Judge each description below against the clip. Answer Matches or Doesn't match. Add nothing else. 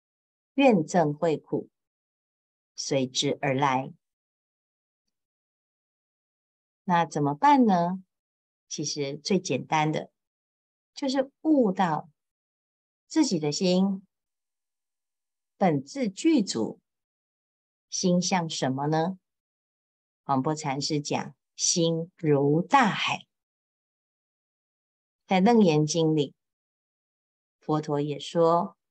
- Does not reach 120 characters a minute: Matches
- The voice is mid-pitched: Matches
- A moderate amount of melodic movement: Matches